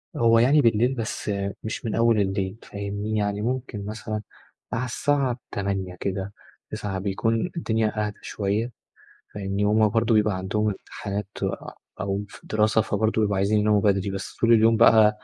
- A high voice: No, low, 105 Hz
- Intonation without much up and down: Yes, narrow, 2.1 semitones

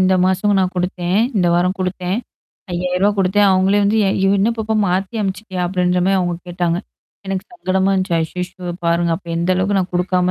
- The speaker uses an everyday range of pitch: No, narrow, 1.4 semitones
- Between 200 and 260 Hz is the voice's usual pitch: No, medium, 185 Hz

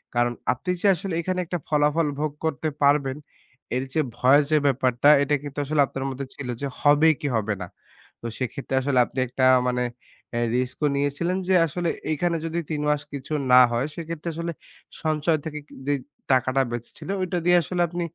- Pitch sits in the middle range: Yes, medium, 145 Hz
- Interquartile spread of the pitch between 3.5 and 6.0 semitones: Yes, average, 3.9 semitones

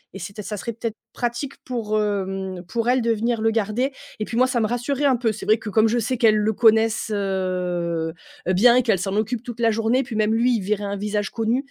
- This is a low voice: No, high, 220 Hz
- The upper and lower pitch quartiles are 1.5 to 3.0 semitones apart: Yes, narrow, 2.6 semitones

